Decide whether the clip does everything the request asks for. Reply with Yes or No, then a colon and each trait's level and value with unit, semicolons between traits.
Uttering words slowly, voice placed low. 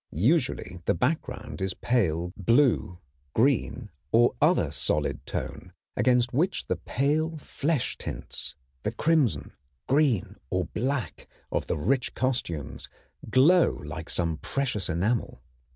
Yes: slow, 120 wpm; low, 120 Hz